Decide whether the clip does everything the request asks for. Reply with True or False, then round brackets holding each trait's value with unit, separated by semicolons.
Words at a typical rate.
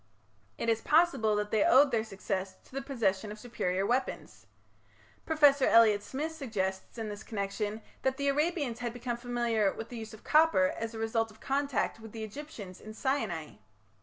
True (180 wpm)